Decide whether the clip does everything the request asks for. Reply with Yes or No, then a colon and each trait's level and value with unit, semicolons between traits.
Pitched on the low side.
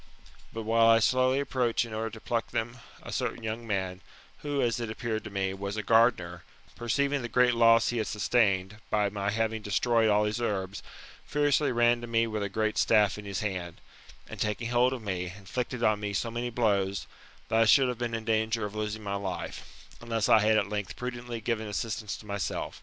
Yes: low, 110 Hz